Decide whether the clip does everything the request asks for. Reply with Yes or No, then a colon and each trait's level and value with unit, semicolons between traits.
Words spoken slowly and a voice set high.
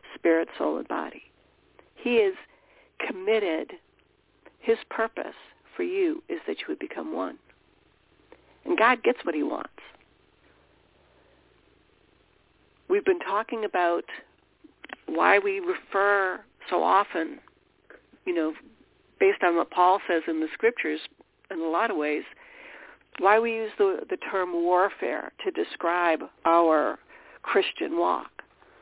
Yes: slow, 125 wpm; high, 230 Hz